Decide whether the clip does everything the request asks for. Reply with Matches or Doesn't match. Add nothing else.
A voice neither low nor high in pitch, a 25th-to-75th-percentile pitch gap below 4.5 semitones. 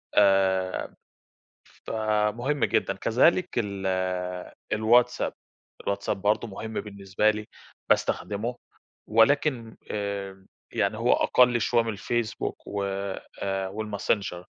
Doesn't match